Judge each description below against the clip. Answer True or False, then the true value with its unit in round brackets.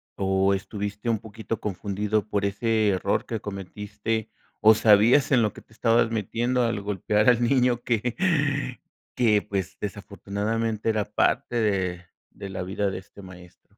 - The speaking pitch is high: False (105 Hz)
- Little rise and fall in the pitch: True (2.3 semitones)